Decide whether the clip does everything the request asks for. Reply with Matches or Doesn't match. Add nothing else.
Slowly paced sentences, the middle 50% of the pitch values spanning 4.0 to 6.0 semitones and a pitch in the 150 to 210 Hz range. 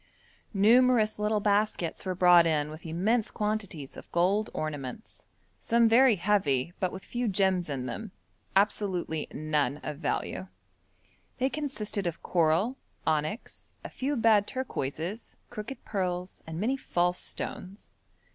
Matches